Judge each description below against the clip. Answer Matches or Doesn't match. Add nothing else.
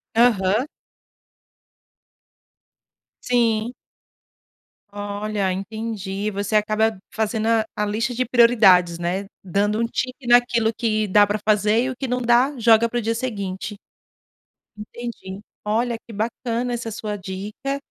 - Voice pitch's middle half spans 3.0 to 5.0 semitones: Doesn't match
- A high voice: Matches